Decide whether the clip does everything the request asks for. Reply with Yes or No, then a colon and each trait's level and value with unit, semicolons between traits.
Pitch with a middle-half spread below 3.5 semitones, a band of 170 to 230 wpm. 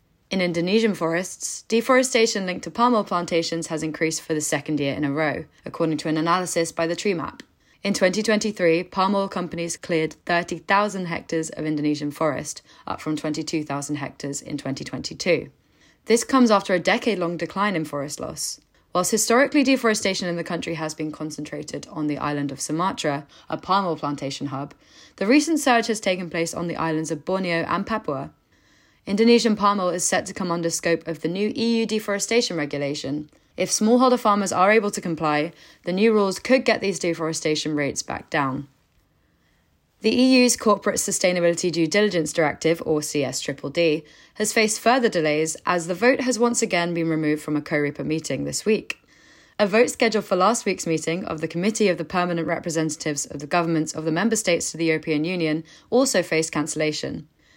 No: average, 4.8 semitones; average, 180 wpm